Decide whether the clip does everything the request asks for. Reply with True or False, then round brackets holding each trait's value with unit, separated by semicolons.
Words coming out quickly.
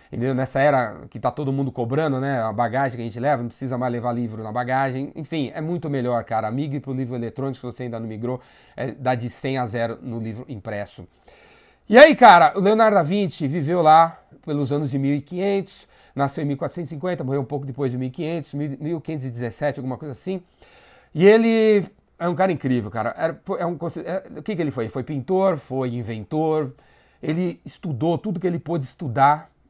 True (200 wpm)